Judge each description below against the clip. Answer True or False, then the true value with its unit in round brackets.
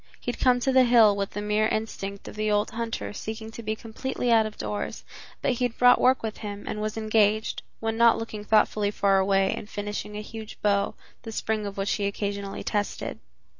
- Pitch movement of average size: False (1.6 semitones)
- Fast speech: True (215 wpm)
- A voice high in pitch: True (215 Hz)